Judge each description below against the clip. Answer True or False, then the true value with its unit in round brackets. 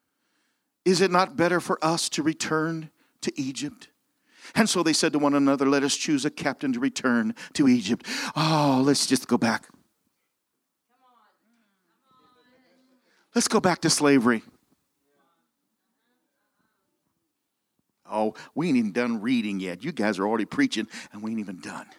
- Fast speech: False (145 wpm)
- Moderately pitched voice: True (175 Hz)